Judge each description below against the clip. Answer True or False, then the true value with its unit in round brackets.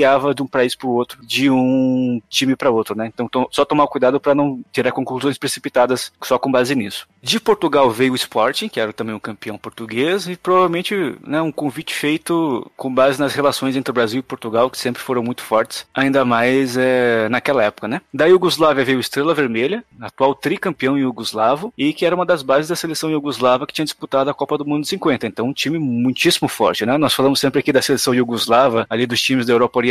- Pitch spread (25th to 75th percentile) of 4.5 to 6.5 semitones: False (2.9 semitones)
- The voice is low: True (130 Hz)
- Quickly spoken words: True (220 wpm)